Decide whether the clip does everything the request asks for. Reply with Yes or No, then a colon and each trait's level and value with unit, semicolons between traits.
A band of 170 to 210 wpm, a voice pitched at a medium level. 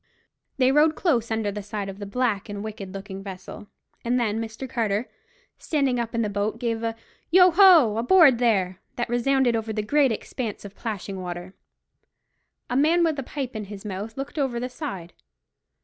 No: average, 185 wpm; high, 230 Hz